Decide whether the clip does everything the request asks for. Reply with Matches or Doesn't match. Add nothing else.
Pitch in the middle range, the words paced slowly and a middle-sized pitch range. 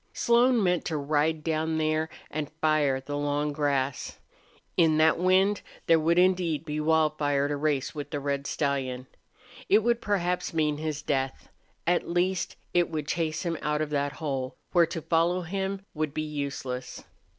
Doesn't match